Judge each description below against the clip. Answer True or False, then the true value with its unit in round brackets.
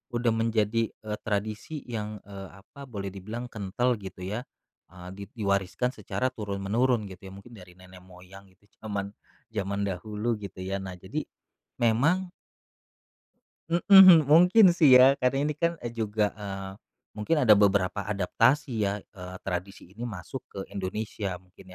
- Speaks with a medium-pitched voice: False (105 Hz)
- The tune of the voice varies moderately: True (4.0 semitones)